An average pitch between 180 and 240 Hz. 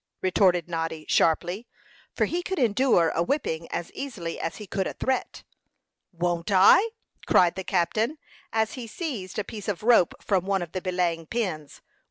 Yes: high, 190 Hz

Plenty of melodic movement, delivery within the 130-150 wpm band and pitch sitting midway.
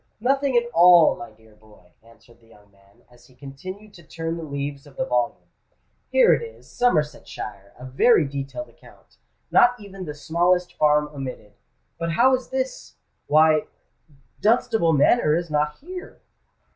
Yes: wide, 7.8 semitones; average, 145 wpm; medium, 155 Hz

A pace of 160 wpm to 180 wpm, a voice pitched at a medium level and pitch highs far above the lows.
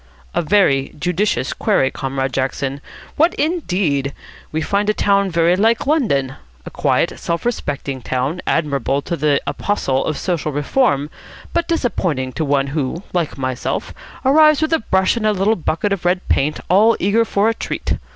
Yes: average, 165 wpm; medium, 170 Hz; wide, 7.1 semitones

